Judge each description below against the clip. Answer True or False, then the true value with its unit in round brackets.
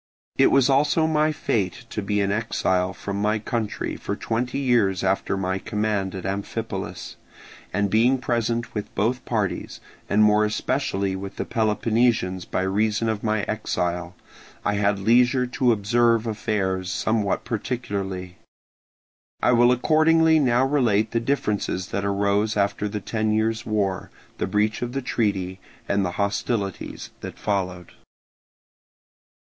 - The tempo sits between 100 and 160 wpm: True (140 wpm)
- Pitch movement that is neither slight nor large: True (3.2 semitones)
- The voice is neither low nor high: False (105 Hz)